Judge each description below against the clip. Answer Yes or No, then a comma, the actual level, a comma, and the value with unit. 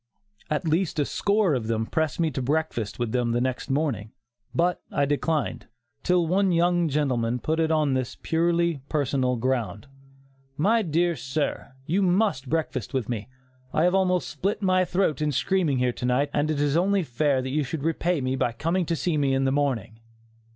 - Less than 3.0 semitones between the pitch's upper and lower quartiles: No, average, 4.8 semitones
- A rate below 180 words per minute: No, average, 190 wpm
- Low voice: No, medium, 150 Hz